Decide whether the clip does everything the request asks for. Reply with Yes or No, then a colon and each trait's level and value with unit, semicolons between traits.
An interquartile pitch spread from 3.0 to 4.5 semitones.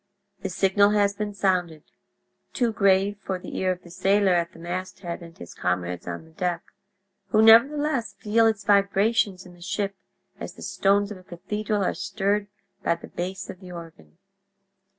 No: narrow, 2.6 semitones